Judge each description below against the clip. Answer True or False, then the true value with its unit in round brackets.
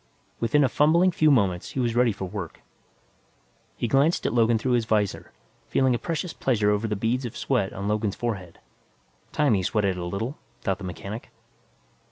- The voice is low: True (115 Hz)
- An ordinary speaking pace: True (185 wpm)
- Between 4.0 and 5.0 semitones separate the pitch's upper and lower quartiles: True (4.5 semitones)